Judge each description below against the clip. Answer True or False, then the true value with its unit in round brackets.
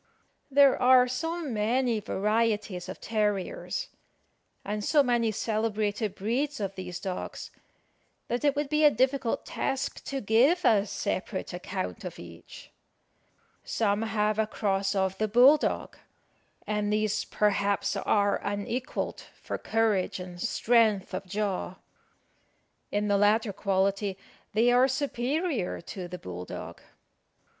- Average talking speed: False (130 wpm)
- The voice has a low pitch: False (215 Hz)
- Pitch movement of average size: True (3.8 semitones)